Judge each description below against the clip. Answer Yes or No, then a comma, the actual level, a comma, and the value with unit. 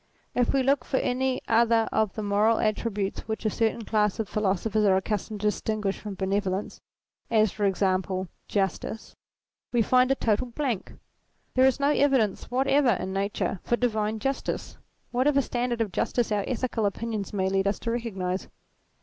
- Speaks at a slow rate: No, average, 170 wpm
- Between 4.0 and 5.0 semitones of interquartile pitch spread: No, average, 3.5 semitones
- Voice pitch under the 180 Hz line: No, high, 220 Hz